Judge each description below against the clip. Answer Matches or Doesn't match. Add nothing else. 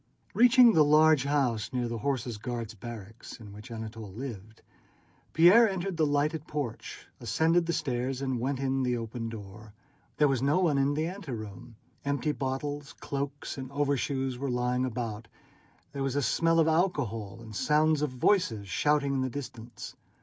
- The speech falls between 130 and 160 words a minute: Doesn't match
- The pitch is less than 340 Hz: Matches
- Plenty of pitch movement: Doesn't match